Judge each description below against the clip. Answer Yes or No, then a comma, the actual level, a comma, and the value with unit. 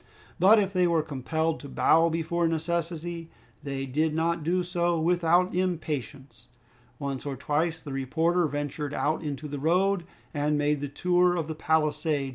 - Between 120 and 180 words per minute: Yes, average, 160 wpm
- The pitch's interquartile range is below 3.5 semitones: Yes, average, 2.9 semitones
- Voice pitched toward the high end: No, medium, 160 Hz